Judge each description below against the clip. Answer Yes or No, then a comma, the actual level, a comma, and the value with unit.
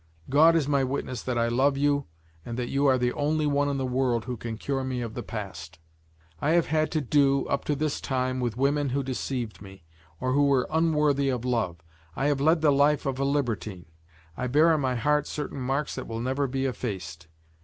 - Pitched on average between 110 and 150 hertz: Yes, low, 135 Hz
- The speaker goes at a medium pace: No, fast, 220 wpm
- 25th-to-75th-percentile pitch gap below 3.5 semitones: Yes, average, 2.8 semitones